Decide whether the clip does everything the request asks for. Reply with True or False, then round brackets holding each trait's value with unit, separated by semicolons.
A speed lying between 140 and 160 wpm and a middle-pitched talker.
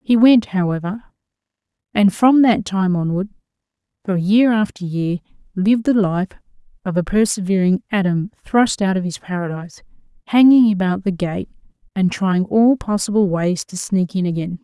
False (150 wpm; 195 Hz)